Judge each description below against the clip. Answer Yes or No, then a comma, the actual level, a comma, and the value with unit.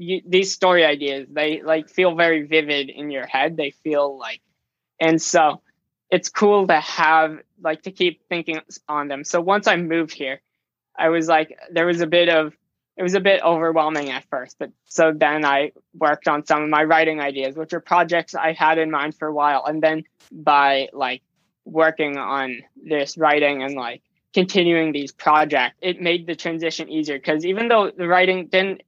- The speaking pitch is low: No, medium, 160 Hz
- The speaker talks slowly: No, average, 190 wpm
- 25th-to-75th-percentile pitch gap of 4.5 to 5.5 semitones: No, average, 2.8 semitones